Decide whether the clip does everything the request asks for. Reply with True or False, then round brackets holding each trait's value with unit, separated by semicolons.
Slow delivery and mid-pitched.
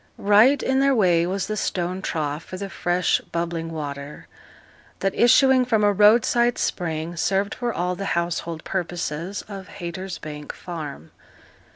False (145 wpm; 180 Hz)